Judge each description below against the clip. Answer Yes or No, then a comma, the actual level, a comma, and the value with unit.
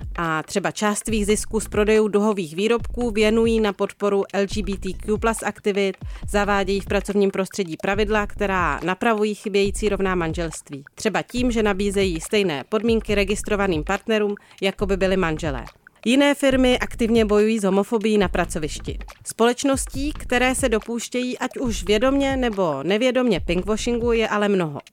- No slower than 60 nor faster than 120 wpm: No, average, 135 wpm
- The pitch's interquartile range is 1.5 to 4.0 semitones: Yes, average, 2.7 semitones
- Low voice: No, high, 205 Hz